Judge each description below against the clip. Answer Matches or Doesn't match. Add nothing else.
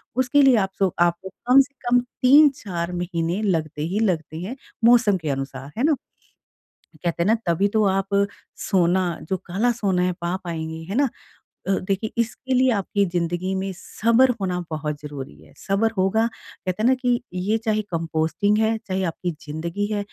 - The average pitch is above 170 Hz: Matches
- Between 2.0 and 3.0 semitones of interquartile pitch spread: Doesn't match